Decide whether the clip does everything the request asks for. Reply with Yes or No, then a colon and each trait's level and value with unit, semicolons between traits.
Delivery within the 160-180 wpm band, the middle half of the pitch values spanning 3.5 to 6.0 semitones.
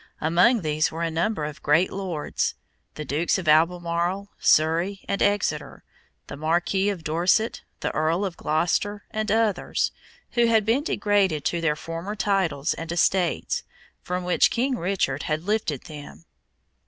No: average, 150 wpm; average, 4.2 semitones